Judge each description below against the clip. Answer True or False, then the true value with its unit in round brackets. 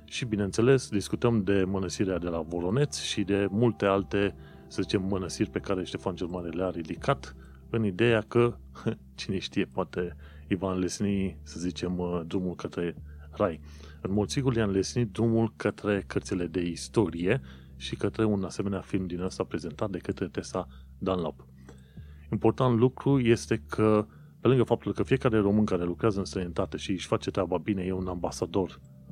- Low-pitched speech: True (95 Hz)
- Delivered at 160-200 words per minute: True (165 wpm)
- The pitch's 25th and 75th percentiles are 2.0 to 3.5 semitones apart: False (3.9 semitones)